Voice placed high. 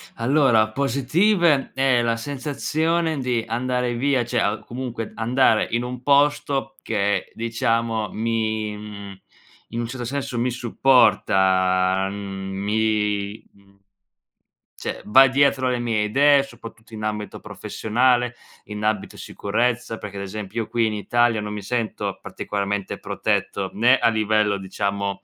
No: low, 115 Hz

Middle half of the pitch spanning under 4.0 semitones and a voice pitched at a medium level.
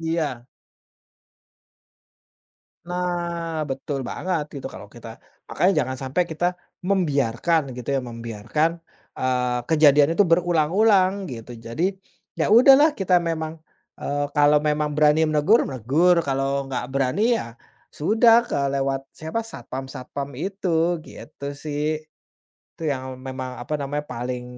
No: average, 4.5 semitones; medium, 150 Hz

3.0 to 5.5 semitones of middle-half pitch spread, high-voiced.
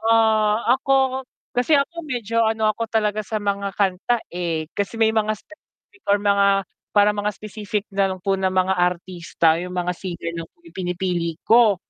Yes: average, 3.5 semitones; high, 205 Hz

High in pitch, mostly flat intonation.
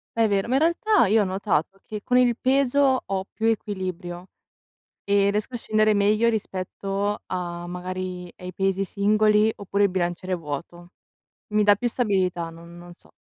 No: high, 200 Hz; average, 3.0 semitones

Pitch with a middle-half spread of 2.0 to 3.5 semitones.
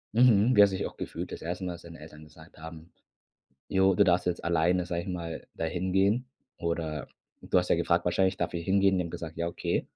Yes: narrow, 2.4 semitones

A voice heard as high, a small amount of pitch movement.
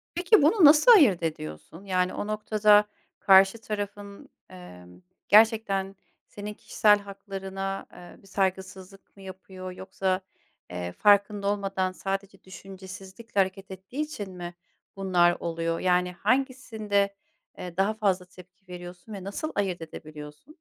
Yes: high, 195 Hz; narrow, 2.2 semitones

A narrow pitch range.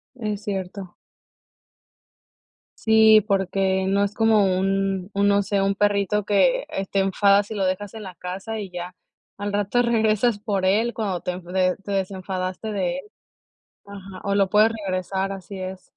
Yes: narrow, 1.7 semitones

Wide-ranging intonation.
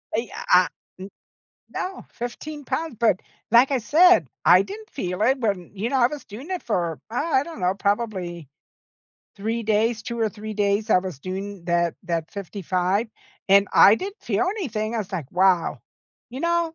Yes: wide, 5.9 semitones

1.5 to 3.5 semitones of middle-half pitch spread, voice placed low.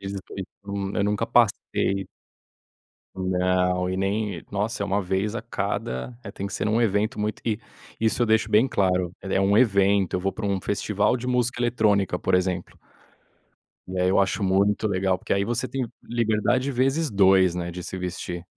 Yes: average, 2.9 semitones; low, 100 Hz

